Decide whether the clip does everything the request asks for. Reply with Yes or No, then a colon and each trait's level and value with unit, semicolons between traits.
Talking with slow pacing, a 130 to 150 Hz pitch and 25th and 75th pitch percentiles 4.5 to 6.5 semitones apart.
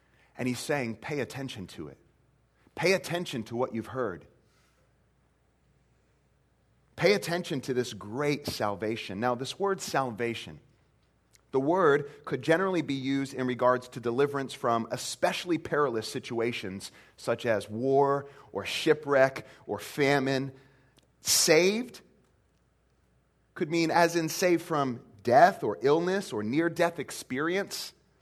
Yes: slow, 125 wpm; low, 135 Hz; average, 5.2 semitones